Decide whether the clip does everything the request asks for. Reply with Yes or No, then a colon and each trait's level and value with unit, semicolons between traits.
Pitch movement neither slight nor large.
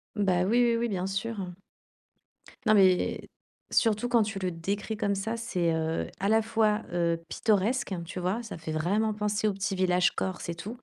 Yes: average, 3.4 semitones